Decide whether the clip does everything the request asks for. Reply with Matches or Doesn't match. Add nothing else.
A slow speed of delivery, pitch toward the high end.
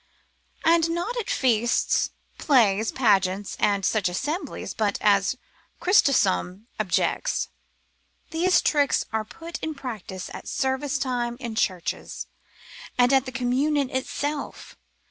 Matches